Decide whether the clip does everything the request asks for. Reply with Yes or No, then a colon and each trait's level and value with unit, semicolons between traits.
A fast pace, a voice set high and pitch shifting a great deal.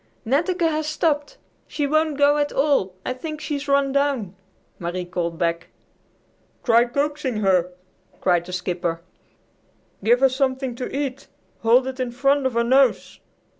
No: average, 150 wpm; very high, 260 Hz; wide, 6.3 semitones